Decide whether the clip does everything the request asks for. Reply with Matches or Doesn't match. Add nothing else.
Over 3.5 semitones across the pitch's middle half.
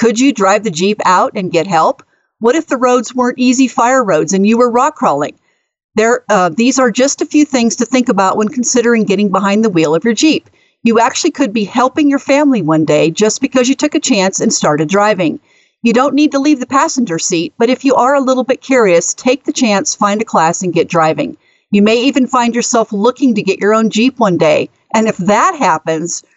Matches